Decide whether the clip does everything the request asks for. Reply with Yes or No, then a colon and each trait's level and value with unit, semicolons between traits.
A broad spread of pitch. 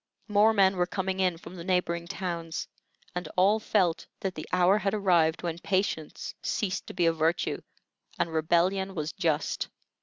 No: narrow, 2.4 semitones